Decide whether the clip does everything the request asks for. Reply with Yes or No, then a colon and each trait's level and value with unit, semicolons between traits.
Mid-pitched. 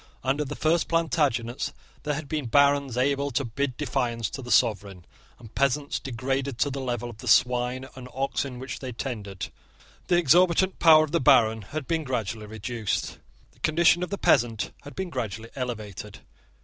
No: low, 130 Hz